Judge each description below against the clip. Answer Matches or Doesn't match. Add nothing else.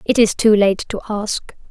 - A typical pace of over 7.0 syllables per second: Doesn't match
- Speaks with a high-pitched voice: Matches